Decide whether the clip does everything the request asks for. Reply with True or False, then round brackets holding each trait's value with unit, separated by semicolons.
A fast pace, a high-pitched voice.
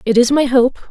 True (265 wpm; 250 Hz)